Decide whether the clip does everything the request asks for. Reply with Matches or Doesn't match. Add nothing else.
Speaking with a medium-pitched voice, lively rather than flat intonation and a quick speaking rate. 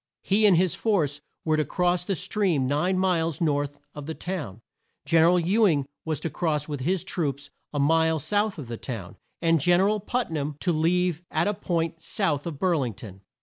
Doesn't match